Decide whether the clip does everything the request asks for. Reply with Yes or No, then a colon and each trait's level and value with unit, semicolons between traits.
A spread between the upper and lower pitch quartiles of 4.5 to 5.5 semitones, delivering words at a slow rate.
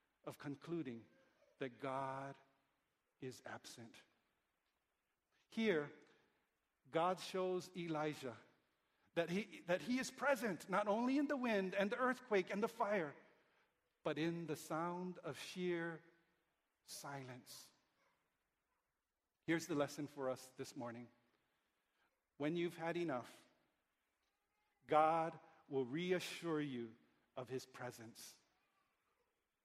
Yes: average, 5.1 semitones; slow, 105 wpm